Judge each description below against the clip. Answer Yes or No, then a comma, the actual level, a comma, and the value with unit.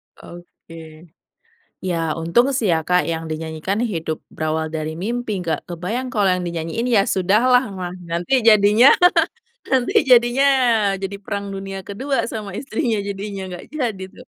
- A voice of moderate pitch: No, high, 195 Hz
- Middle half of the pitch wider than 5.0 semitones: Yes, wide, 5.5 semitones